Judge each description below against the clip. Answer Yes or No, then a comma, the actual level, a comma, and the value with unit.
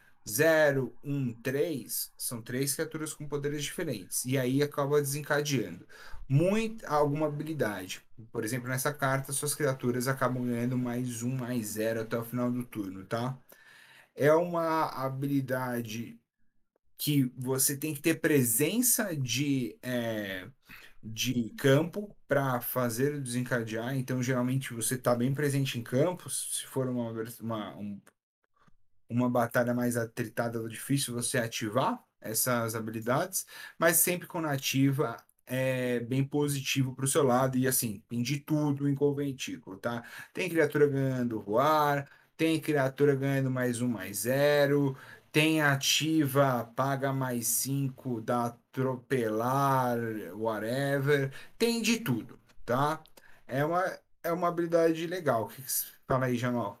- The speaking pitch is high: No, low, 130 Hz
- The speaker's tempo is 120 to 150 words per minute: Yes, average, 135 wpm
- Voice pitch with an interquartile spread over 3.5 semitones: No, average, 3.1 semitones